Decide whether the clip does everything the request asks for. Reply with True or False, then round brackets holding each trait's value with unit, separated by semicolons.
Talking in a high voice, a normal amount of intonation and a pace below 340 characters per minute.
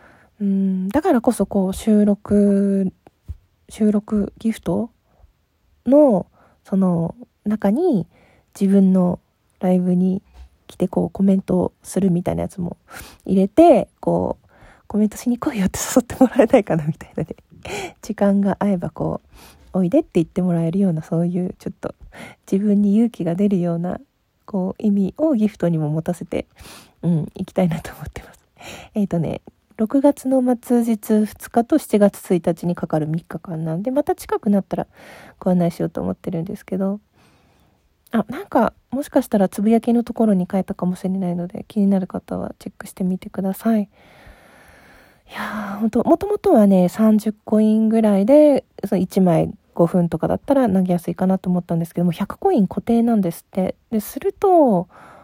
True (195 Hz; 3.7 semitones; 320 characters per minute)